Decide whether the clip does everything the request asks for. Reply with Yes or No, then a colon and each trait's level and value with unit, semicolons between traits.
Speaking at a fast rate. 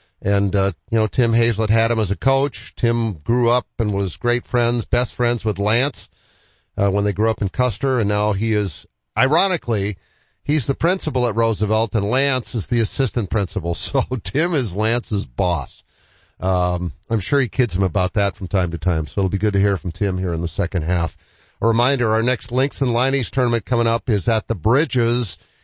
Yes: fast, 210 wpm